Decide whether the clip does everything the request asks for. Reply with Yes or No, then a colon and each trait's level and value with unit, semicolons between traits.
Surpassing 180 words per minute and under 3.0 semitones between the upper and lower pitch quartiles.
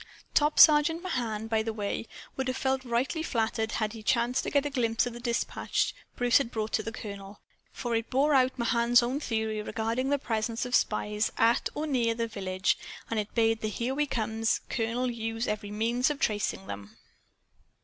Yes: average, 195 wpm; narrow, 2.6 semitones